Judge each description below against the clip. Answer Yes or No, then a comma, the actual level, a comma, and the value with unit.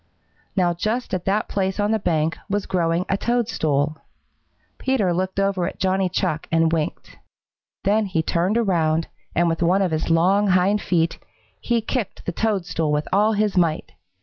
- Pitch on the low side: No, medium, 185 Hz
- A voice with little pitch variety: No, average, 3.7 semitones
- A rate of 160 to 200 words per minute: Yes, average, 170 wpm